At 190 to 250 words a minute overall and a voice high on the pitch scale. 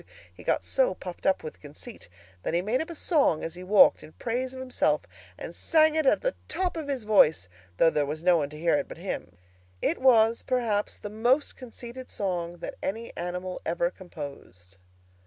Yes: average, 200 wpm; high, 205 Hz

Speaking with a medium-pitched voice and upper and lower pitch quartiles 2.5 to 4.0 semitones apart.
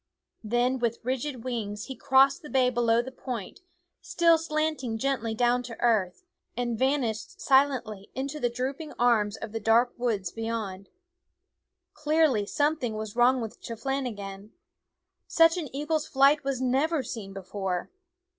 No: high, 245 Hz; average, 3.7 semitones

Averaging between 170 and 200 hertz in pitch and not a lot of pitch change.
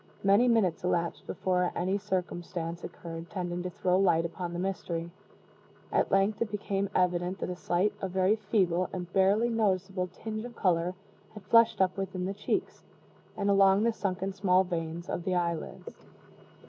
Yes: medium, 185 Hz; narrow, 2.1 semitones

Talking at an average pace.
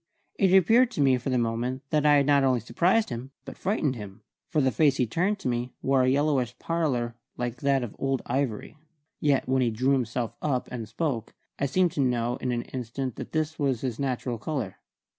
No: fast, 215 wpm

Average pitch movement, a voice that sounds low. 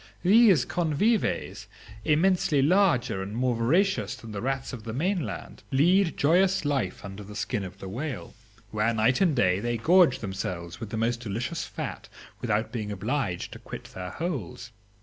No: wide, 8.0 semitones; low, 125 Hz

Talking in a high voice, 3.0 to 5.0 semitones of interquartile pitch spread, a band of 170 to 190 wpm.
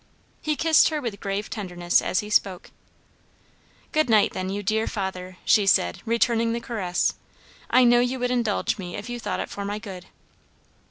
Yes: high, 210 Hz; average, 4.0 semitones; average, 180 wpm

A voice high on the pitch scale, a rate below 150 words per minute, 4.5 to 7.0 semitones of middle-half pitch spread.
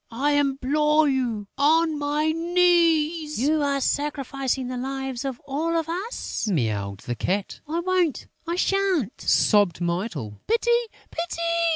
Yes: very high, 290 Hz; slow, 135 wpm; average, 5.2 semitones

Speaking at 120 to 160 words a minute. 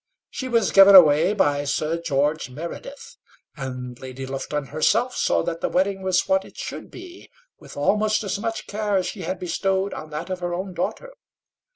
No: average, 185 wpm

